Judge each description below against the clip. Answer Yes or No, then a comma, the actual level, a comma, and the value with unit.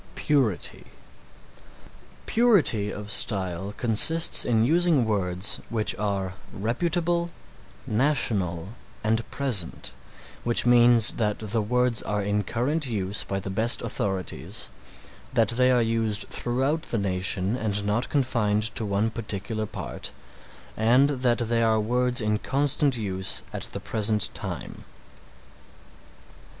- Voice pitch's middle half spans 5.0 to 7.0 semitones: No, average, 3.4 semitones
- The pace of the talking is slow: Yes, slow, 120 wpm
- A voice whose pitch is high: No, low, 110 Hz